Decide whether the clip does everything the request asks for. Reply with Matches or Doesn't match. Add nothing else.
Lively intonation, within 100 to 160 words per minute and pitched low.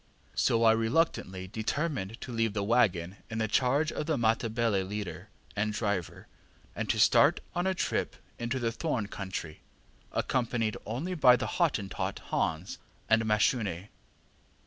Doesn't match